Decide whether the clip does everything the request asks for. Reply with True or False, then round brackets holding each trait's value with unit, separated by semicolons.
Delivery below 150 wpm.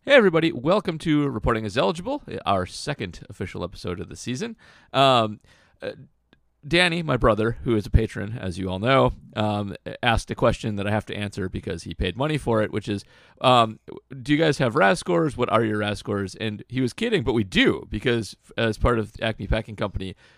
False (205 wpm)